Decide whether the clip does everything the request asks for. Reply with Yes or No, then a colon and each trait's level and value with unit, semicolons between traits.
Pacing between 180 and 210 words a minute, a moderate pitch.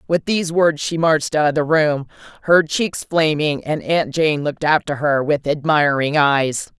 Yes: average, 185 wpm; medium, 150 Hz